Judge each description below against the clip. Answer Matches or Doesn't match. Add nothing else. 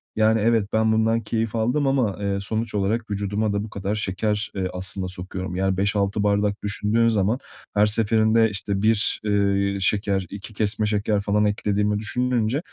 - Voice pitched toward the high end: Doesn't match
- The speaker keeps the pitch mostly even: Matches